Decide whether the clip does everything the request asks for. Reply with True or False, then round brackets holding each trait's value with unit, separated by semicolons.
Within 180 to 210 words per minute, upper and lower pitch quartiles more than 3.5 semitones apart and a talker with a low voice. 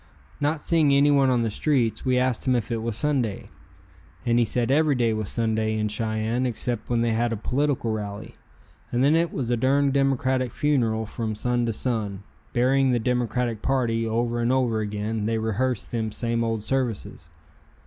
False (185 wpm; 2.7 semitones; 120 Hz)